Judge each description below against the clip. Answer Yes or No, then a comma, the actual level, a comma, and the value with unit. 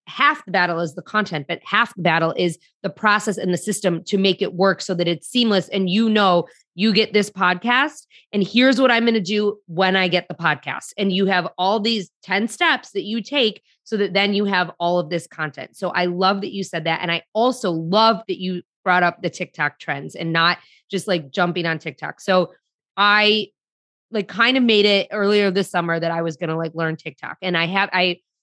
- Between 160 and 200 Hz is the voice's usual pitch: Yes, high, 190 Hz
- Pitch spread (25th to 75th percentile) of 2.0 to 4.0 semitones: Yes, average, 3.3 semitones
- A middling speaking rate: No, fast, 230 wpm